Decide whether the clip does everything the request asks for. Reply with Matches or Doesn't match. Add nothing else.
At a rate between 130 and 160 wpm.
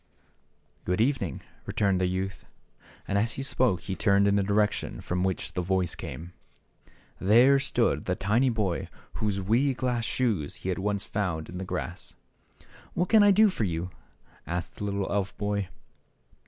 Doesn't match